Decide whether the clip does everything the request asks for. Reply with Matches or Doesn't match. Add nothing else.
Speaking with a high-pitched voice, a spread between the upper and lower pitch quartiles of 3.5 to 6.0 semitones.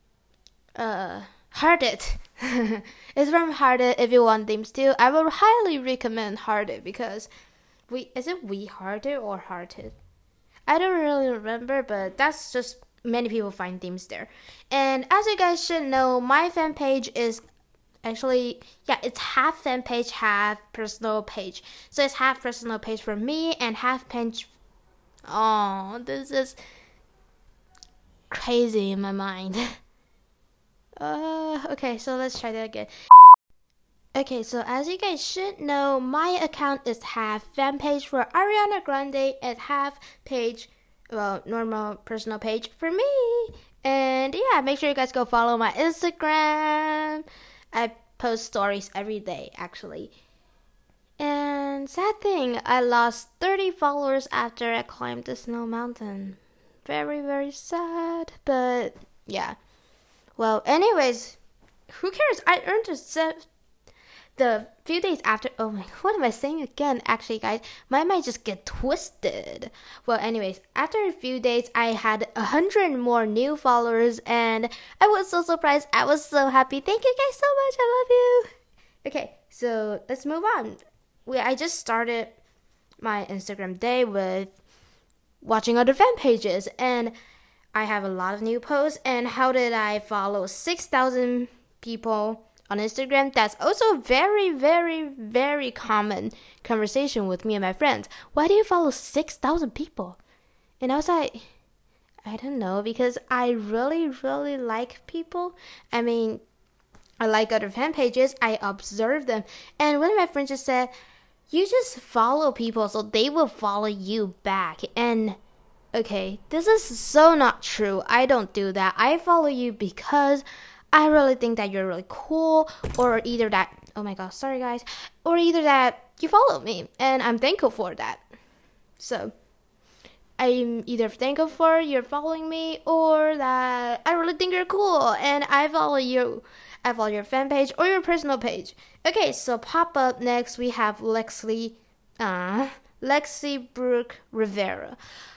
Matches